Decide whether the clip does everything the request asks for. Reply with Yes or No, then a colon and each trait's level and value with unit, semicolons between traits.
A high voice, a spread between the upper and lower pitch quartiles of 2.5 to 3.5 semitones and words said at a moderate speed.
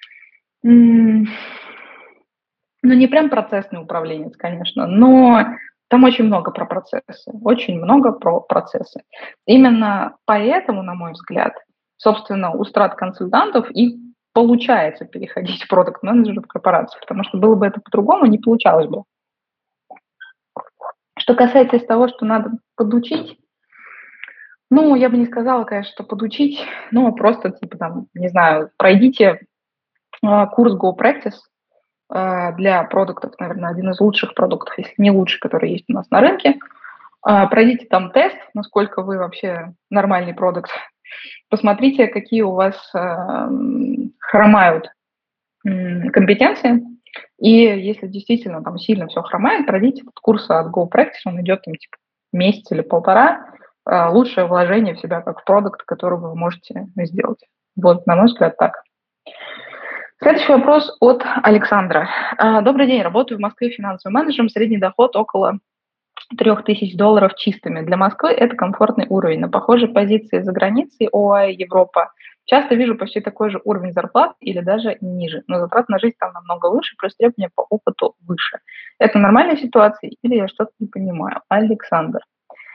No: high, 215 Hz; average, 4.2 semitones; average, 135 wpm